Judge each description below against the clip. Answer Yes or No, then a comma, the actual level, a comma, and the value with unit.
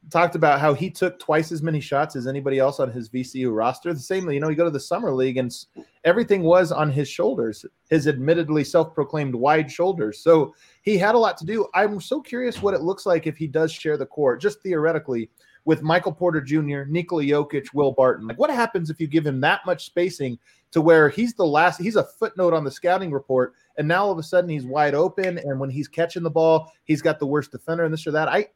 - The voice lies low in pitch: No, medium, 160 Hz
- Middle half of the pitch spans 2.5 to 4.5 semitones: Yes, average, 3.8 semitones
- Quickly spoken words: Yes, fast, 240 wpm